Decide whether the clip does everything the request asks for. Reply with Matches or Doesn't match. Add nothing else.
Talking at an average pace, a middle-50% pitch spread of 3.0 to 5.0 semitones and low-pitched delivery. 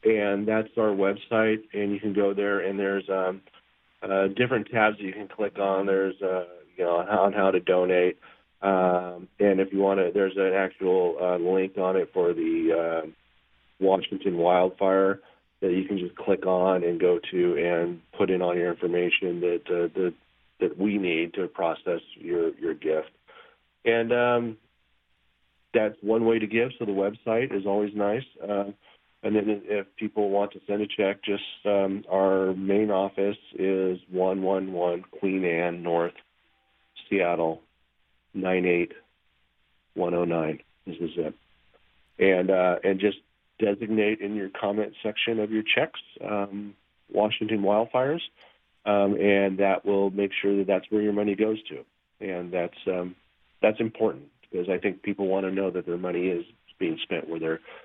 Doesn't match